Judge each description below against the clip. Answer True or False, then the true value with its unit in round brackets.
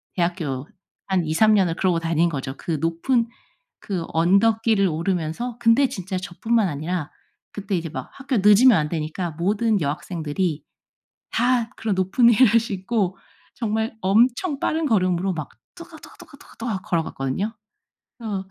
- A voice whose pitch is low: False (190 Hz)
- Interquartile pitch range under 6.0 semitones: True (5.3 semitones)